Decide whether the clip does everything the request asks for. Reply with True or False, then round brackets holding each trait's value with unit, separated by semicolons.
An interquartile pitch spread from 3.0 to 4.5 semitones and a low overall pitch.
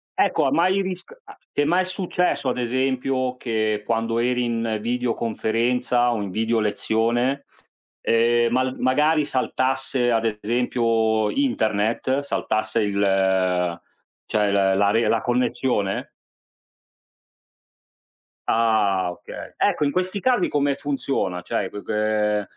True (3.6 semitones; 115 Hz)